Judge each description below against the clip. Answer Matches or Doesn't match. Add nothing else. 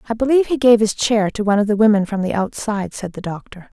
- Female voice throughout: Matches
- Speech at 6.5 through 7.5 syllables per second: Matches